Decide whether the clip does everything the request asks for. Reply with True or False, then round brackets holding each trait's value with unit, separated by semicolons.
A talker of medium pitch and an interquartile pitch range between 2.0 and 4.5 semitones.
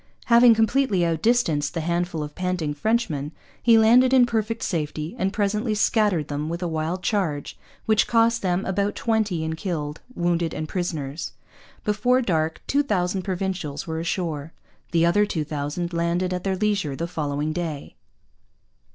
False (175 Hz; 5.0 semitones)